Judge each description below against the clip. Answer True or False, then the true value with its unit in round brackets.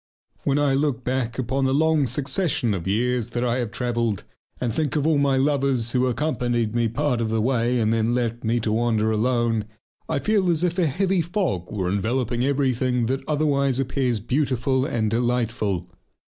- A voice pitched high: False (125 Hz)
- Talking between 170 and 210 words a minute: True (185 wpm)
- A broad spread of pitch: False (3.3 semitones)